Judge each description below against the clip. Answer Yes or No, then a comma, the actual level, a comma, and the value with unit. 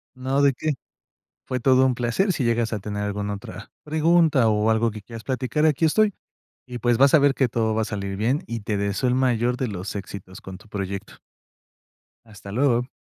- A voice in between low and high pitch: No, low, 120 Hz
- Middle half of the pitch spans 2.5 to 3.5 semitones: No, average, 4.2 semitones